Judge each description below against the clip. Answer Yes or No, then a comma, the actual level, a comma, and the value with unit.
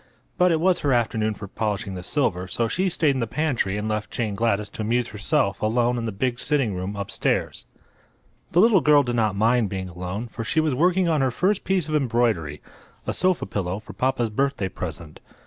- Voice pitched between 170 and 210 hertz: No, low, 115 Hz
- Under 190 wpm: No, fast, 205 wpm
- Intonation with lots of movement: Yes, wide, 6.1 semitones